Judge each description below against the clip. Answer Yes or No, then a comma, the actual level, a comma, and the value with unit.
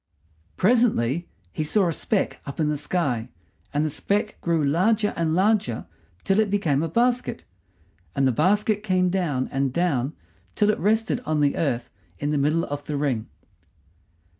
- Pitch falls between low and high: Yes, medium, 165 Hz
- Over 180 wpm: No, average, 165 wpm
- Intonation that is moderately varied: No, wide, 6.2 semitones